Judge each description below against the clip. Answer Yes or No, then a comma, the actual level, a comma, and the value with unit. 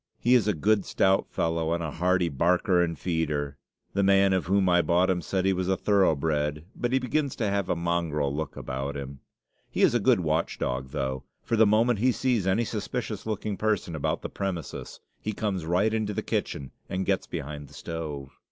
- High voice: No, very low, 90 Hz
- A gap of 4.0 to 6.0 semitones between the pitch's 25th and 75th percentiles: Yes, average, 4.8 semitones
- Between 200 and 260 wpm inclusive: Yes, fast, 205 wpm